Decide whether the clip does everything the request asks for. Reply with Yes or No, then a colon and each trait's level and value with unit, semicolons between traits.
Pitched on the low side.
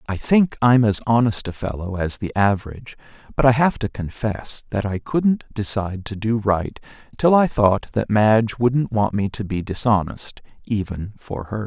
Yes: low, 110 Hz